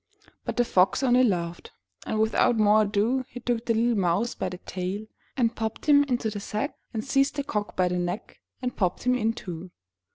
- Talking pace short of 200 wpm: No, fast, 205 wpm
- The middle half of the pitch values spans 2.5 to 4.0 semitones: No, average, 4.5 semitones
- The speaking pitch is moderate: No, high, 220 Hz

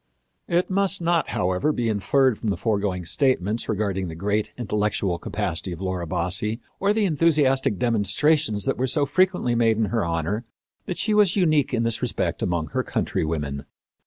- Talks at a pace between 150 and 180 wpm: Yes, average, 170 wpm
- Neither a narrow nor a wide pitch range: No, wide, 8.0 semitones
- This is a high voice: No, low, 110 Hz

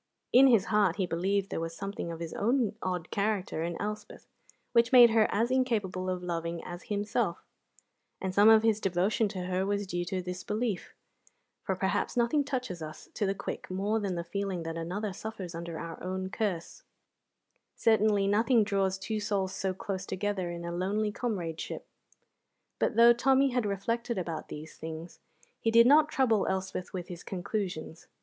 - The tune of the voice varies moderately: Yes, average, 3.5 semitones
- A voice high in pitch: Yes, high, 195 Hz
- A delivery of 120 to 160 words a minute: No, average, 175 wpm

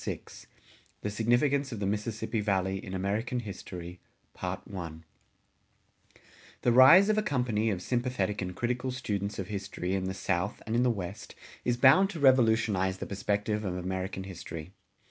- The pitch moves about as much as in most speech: Yes, average, 4.5 semitones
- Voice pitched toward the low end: Yes, low, 105 Hz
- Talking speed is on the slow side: No, average, 150 wpm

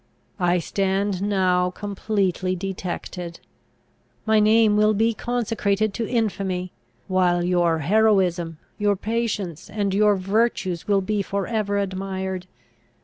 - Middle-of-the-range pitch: No, high, 195 Hz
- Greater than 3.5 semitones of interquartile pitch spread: No, narrow, 2.5 semitones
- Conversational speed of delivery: No, slow, 115 wpm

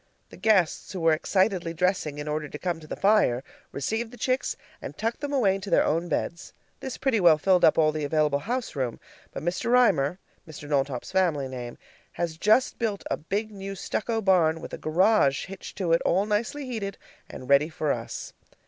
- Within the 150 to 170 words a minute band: No, average, 200 wpm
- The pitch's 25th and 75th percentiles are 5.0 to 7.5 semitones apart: Yes, wide, 5.6 semitones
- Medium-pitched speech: Yes, medium, 180 Hz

